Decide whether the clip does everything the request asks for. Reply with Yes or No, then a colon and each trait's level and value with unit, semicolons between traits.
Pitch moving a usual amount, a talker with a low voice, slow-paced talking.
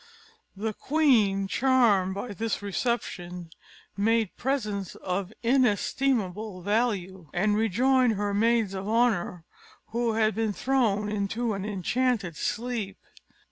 No: average, 3.4 semitones; high, 215 Hz; slow, 110 wpm